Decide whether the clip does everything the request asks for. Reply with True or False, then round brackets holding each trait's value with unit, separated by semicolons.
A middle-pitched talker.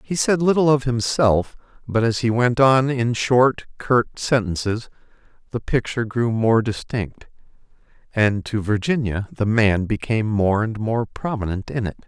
False (115 Hz)